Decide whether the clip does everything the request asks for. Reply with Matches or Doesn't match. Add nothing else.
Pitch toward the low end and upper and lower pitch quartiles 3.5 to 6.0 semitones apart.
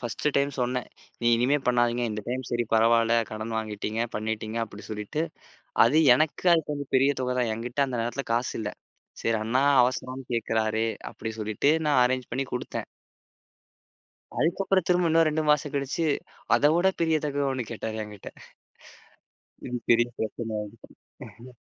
Matches